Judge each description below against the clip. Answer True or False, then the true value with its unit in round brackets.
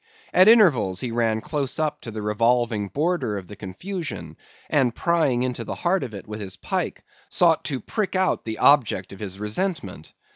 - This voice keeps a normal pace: True (185 wpm)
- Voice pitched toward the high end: False (120 Hz)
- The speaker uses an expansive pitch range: True (7.7 semitones)